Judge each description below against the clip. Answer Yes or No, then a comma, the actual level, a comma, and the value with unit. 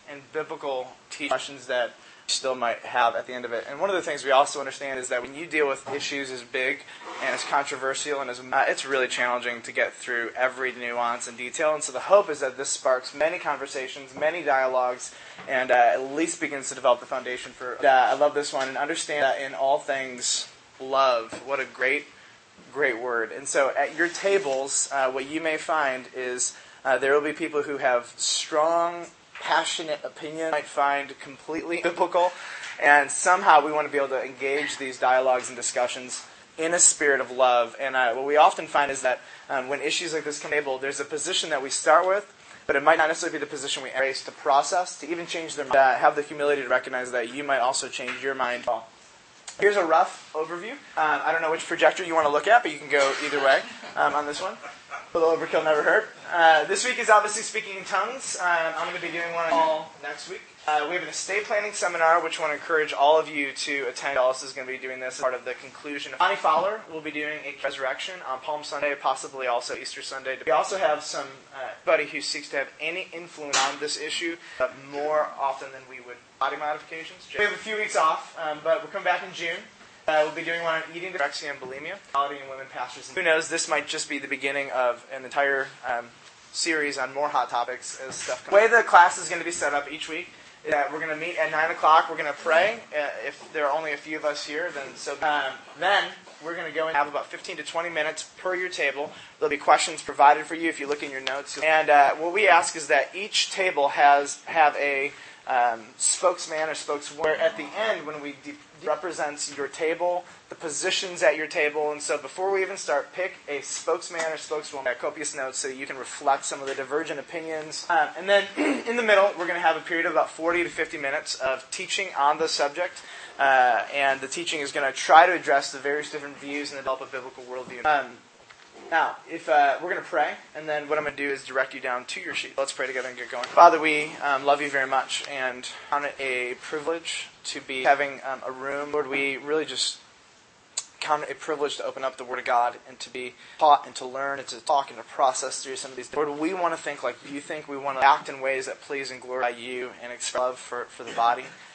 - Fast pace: Yes, fast, 240 wpm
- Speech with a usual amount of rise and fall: Yes, average, 3.3 semitones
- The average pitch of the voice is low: No, medium, 145 Hz